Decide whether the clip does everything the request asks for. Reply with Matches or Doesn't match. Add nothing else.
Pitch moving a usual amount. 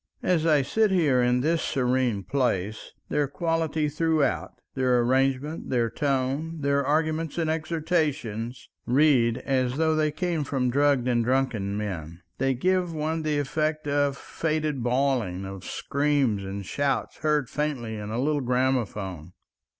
Matches